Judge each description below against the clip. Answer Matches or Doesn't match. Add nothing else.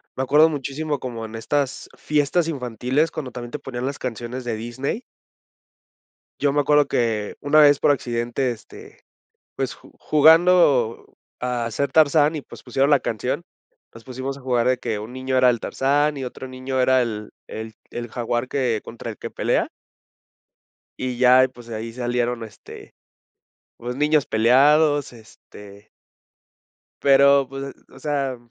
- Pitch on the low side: Matches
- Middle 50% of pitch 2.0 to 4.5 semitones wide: Matches